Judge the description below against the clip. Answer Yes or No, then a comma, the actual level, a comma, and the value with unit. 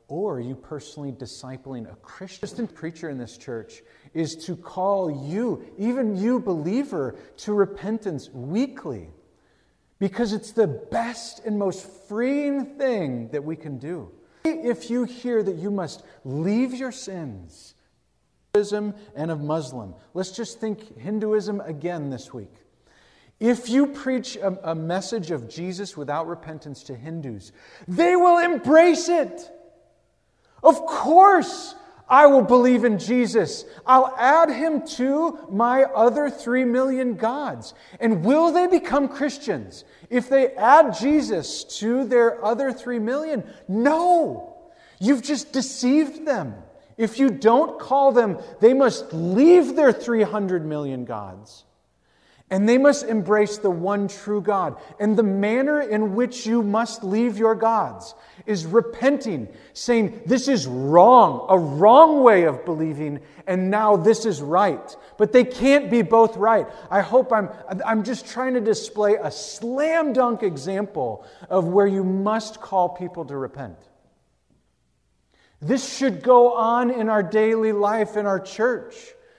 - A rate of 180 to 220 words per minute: No, average, 145 wpm